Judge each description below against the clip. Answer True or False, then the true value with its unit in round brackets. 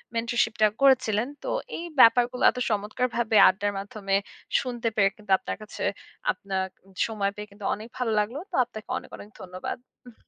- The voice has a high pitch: True (215 Hz)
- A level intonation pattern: False (3.0 semitones)